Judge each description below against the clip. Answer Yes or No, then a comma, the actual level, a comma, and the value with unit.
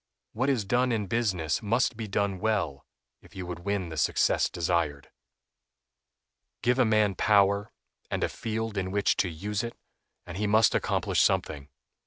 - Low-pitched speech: Yes, low, 100 Hz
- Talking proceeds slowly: No, average, 165 wpm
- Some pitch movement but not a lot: Yes, average, 3.7 semitones